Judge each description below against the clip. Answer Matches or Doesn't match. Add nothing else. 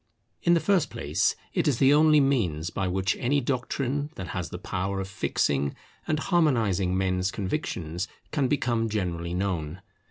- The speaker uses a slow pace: Doesn't match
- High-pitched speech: Doesn't match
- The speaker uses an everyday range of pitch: Doesn't match